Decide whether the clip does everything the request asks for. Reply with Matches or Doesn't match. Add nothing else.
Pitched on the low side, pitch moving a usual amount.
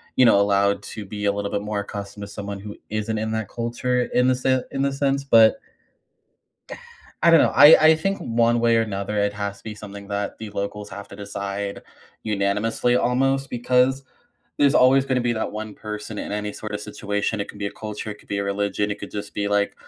Matches